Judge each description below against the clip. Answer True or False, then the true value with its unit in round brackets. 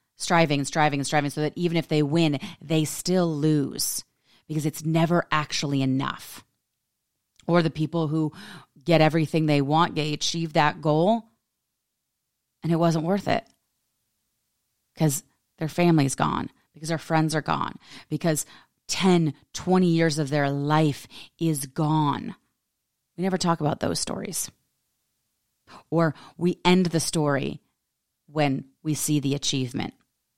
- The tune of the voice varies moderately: False (2.0 semitones)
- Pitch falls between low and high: True (155 Hz)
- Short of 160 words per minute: True (140 wpm)